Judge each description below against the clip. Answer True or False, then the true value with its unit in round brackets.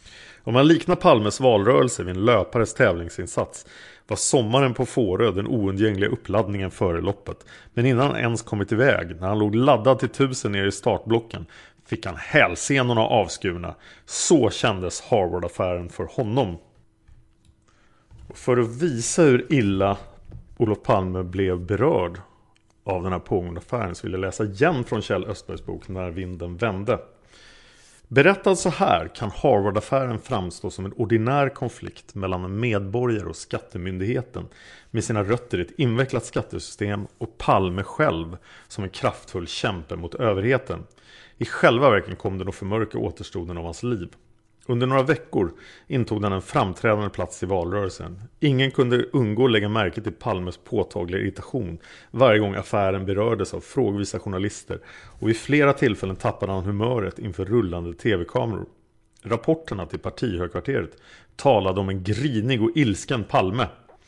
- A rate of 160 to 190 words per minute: False (150 wpm)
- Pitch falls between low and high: False (105 Hz)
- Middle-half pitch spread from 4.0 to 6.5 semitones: True (4.6 semitones)